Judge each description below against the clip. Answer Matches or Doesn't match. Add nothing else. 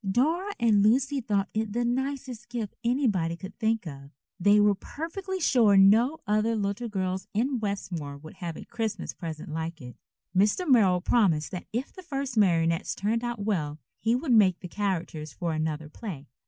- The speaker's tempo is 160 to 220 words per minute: Matches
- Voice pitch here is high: Matches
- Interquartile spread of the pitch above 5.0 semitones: Matches